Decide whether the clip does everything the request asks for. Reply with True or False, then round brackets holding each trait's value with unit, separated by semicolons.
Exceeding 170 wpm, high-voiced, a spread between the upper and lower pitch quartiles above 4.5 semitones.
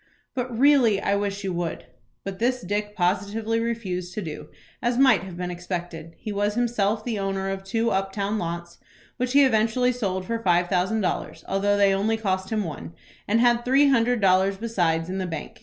False (195 wpm; 200 Hz; 3.7 semitones)